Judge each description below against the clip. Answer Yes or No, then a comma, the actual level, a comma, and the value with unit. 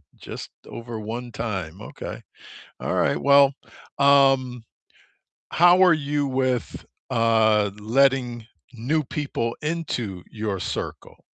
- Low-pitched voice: Yes, low, 125 Hz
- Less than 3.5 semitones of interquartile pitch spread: No, average, 4.0 semitones